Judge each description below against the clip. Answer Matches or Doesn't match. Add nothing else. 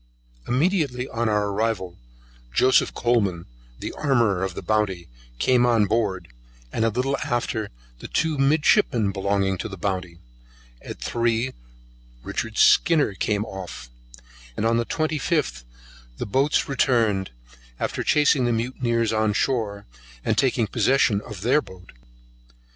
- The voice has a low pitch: Matches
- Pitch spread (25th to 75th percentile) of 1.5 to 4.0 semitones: Doesn't match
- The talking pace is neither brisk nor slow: Doesn't match